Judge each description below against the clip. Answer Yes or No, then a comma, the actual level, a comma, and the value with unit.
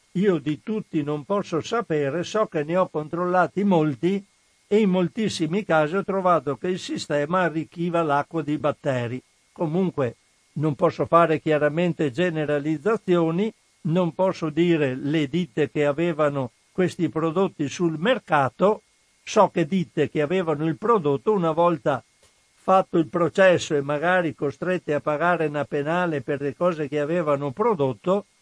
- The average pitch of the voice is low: No, medium, 165 Hz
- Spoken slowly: No, average, 140 wpm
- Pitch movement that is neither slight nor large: Yes, average, 3.5 semitones